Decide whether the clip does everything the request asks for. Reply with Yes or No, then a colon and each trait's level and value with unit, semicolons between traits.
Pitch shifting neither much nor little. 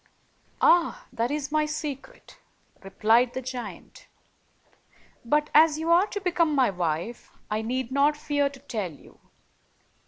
Yes: average, 4.5 semitones